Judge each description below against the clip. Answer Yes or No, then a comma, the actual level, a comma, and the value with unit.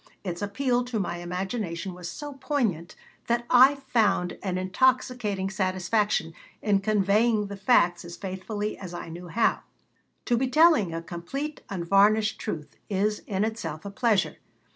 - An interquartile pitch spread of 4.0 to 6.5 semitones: Yes, average, 4.7 semitones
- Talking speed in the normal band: Yes, average, 145 wpm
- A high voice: Yes, high, 200 Hz